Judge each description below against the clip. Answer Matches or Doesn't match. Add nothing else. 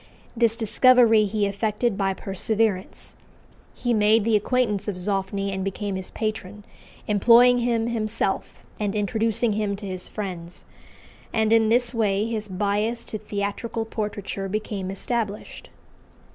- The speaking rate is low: Matches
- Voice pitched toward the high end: Matches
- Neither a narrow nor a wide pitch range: Doesn't match